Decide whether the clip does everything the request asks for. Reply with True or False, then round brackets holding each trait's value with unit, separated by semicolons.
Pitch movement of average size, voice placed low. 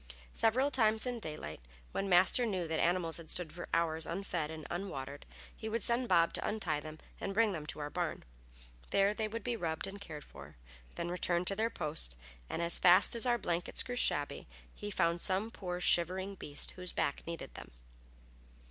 False (4.8 semitones; 180 Hz)